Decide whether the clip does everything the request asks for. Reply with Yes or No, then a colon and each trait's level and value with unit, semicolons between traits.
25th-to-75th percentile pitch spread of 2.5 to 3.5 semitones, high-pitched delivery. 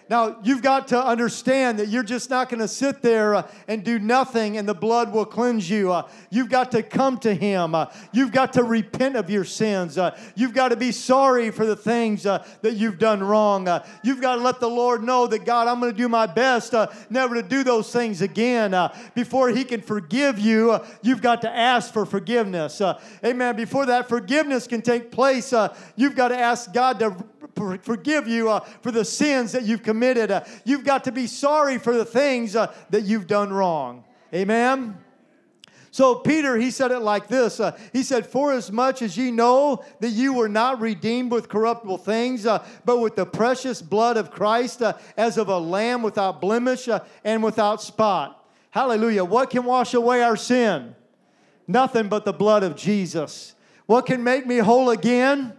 Yes: average, 2.8 semitones; high, 230 Hz